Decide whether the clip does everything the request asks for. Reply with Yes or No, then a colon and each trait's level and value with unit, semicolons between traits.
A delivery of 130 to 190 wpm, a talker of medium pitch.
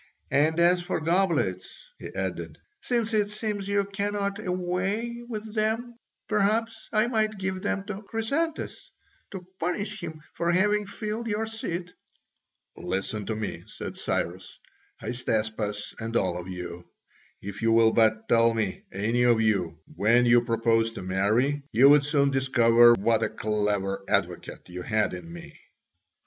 Yes: average, 150 wpm; medium, 145 Hz